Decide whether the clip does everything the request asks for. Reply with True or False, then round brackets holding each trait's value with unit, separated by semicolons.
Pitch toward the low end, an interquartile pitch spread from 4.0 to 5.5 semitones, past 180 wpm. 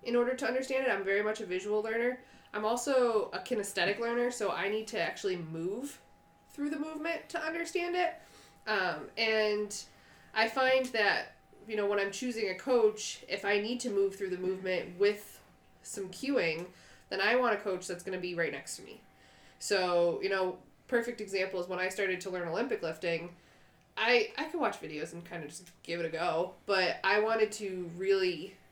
False (205 Hz; 4.8 semitones; 200 wpm)